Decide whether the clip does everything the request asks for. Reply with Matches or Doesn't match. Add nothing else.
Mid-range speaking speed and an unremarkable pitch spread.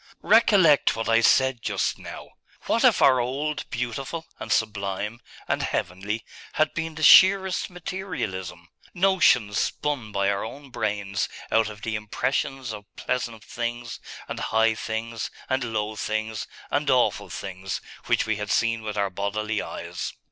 Matches